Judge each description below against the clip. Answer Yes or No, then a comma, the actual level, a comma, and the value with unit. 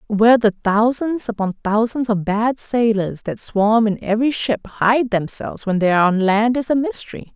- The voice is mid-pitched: No, high, 225 Hz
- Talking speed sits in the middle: Yes, average, 190 wpm